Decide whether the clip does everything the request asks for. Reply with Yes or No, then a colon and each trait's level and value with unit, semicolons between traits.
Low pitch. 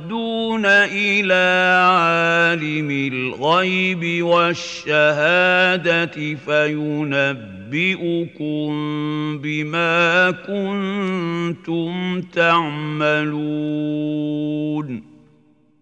No: medium, 165 Hz